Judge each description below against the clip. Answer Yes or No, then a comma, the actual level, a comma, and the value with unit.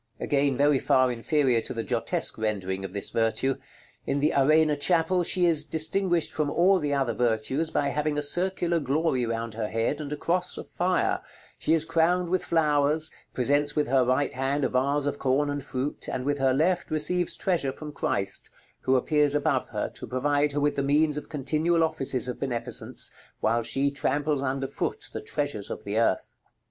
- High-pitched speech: No, medium, 145 Hz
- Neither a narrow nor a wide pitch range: Yes, average, 3.4 semitones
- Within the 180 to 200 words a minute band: Yes, average, 190 wpm